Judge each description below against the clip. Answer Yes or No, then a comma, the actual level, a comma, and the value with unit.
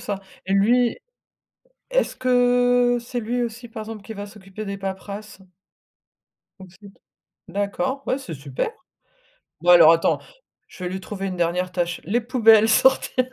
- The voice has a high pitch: Yes, high, 210 Hz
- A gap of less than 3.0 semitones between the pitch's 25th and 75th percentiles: No, average, 4.3 semitones